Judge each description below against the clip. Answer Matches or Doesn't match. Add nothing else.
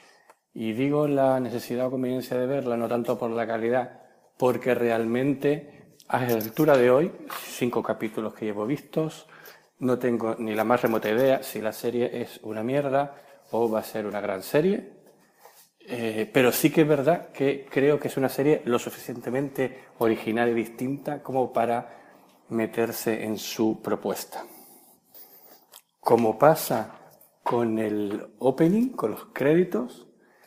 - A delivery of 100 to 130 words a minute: Doesn't match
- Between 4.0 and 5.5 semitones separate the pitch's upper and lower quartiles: Doesn't match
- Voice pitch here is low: Matches